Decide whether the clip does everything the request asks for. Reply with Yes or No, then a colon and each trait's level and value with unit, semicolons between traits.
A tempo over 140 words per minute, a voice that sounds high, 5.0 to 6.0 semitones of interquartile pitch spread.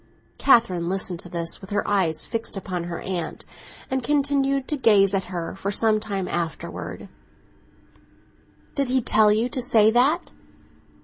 Yes: average, 150 wpm; high, 210 Hz; wide, 5.6 semitones